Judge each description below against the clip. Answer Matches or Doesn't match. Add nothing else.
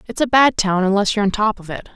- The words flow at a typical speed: Doesn't match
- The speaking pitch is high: Matches